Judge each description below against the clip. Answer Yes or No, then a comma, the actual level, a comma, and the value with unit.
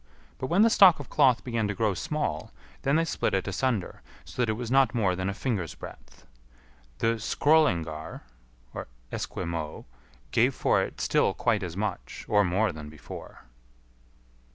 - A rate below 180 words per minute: Yes, average, 160 wpm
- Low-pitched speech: Yes, low, 105 Hz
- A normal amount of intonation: No, wide, 6.7 semitones